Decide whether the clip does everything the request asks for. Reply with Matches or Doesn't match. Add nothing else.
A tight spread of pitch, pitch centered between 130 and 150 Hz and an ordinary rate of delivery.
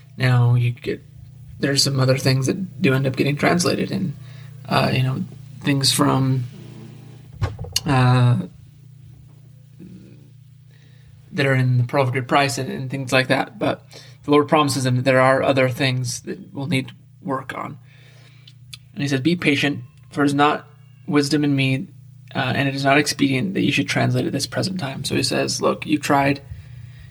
Matches